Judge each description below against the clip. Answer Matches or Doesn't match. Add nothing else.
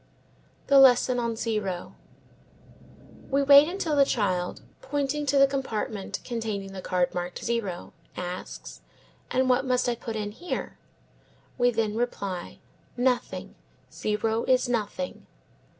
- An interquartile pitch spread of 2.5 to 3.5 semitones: Doesn't match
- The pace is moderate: Doesn't match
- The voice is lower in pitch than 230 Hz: Doesn't match